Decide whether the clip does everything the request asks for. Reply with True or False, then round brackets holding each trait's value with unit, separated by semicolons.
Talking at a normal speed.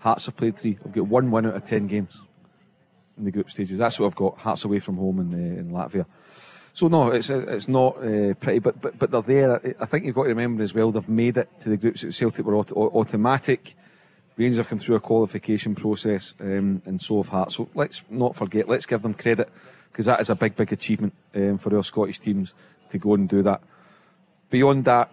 False (230 wpm)